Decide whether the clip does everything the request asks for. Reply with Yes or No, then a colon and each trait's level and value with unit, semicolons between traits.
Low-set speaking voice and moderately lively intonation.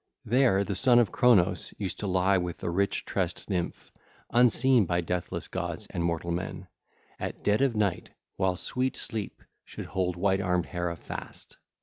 Yes: very low, 95 Hz; average, 3.5 semitones